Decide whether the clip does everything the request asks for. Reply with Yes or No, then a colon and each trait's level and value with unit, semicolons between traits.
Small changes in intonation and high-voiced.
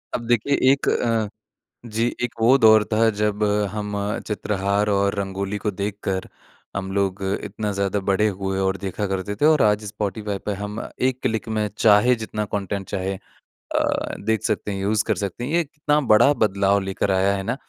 No: narrow, 1.9 semitones; low, 105 Hz